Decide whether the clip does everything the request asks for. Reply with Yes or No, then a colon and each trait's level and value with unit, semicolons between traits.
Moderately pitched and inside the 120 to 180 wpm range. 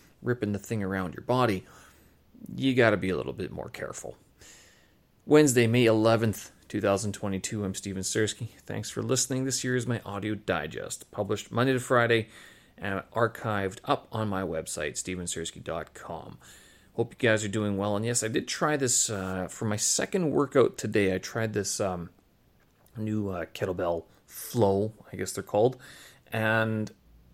No: low, 105 Hz; average, 160 wpm